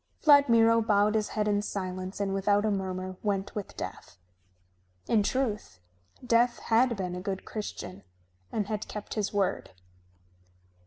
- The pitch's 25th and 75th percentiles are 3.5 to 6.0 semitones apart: No, narrow, 2.6 semitones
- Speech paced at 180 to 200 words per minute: No, average, 145 wpm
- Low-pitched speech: No, high, 205 Hz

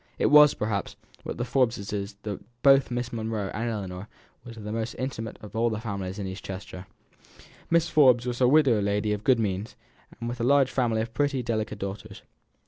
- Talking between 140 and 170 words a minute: No, average, 190 wpm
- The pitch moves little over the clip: No, average, 3.3 semitones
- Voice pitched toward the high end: No, low, 115 Hz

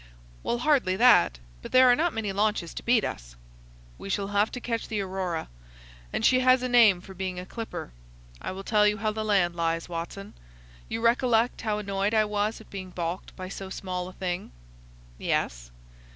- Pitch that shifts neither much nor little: Yes, average, 3.6 semitones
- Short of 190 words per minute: No, average, 195 wpm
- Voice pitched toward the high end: Yes, high, 205 Hz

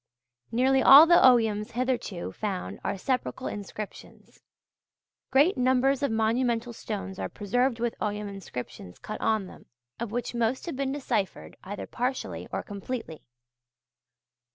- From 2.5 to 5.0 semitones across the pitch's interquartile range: Yes, average, 3.8 semitones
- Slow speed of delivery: Yes, slow, 130 wpm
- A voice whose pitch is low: No, high, 235 Hz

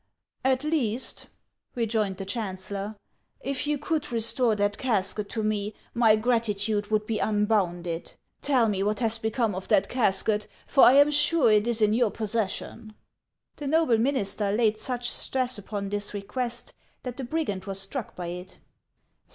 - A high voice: Yes, high, 220 Hz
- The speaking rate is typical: Yes, average, 160 wpm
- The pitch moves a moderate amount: Yes, average, 3.5 semitones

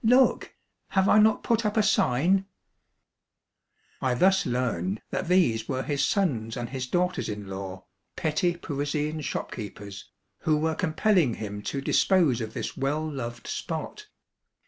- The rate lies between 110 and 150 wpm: Yes, average, 145 wpm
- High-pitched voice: No, medium, 145 Hz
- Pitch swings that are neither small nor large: No, wide, 7.7 semitones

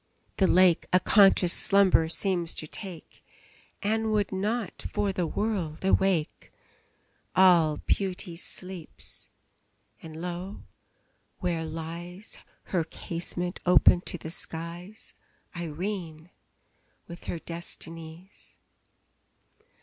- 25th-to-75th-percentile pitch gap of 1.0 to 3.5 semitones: Yes, narrow, 2.6 semitones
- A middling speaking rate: No, slow, 95 wpm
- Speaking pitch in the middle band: Yes, medium, 180 Hz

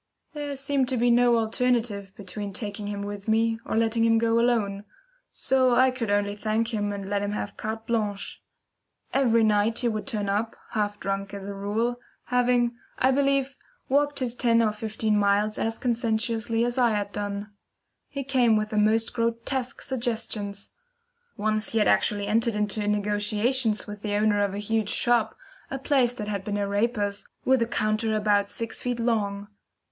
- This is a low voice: No, high, 220 Hz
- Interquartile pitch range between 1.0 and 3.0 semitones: Yes, average, 2.7 semitones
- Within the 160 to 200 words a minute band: Yes, average, 180 wpm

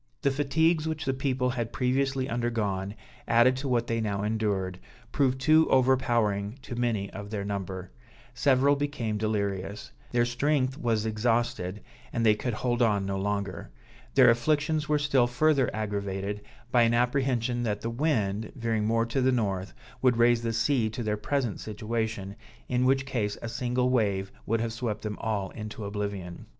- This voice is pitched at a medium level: No, low, 115 Hz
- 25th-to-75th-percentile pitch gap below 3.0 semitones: No, average, 3.7 semitones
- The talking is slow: No, average, 165 wpm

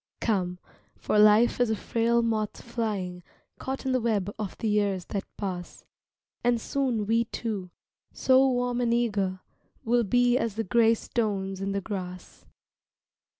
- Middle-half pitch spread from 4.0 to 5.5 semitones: No, average, 3.2 semitones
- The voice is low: No, high, 220 Hz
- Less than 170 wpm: Yes, average, 150 wpm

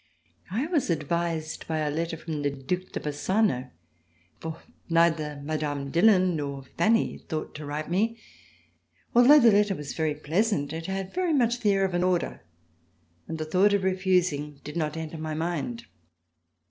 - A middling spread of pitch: Yes, average, 4.3 semitones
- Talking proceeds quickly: No, average, 165 wpm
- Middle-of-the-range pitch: Yes, medium, 165 Hz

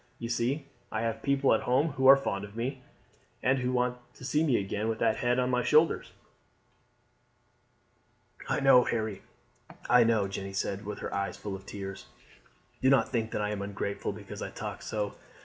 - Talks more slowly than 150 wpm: No, average, 195 wpm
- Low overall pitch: Yes, low, 115 Hz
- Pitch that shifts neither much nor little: Yes, average, 4.1 semitones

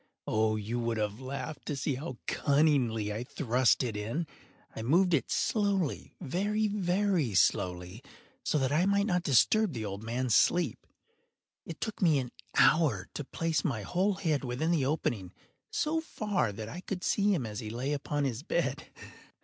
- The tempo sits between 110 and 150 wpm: No, average, 170 wpm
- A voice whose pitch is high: No, medium, 140 Hz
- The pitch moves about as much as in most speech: No, wide, 7.7 semitones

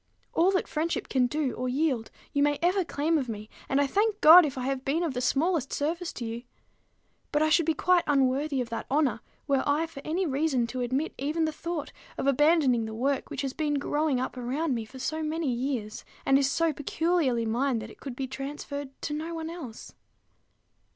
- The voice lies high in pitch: Yes, very high, 285 Hz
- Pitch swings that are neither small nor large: Yes, average, 3.8 semitones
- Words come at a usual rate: No, fast, 215 wpm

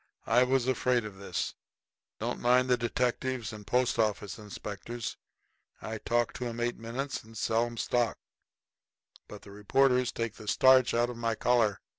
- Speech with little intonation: Yes, narrow, 2.3 semitones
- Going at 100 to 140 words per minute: No, average, 170 wpm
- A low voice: Yes, low, 120 Hz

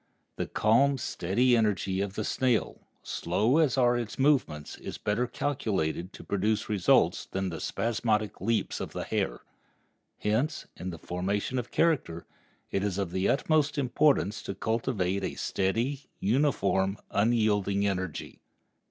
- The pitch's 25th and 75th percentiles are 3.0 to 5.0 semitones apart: Yes, average, 4.5 semitones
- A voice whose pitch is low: Yes, low, 105 Hz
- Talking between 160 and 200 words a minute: No, average, 140 wpm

